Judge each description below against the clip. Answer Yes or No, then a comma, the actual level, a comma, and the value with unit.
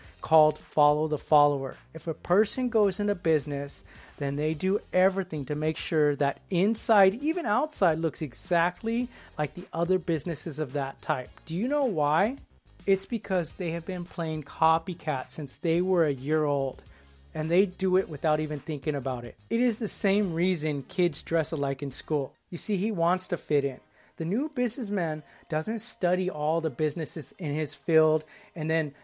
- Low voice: No, medium, 160 Hz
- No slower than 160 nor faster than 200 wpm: Yes, average, 180 wpm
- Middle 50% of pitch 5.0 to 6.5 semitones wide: No, average, 4.0 semitones